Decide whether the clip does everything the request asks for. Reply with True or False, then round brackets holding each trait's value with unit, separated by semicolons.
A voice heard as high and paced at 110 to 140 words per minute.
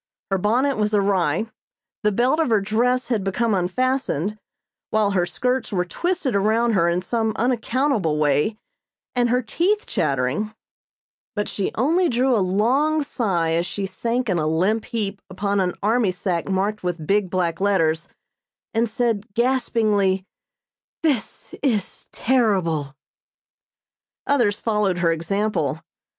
True (210 Hz; 135 wpm)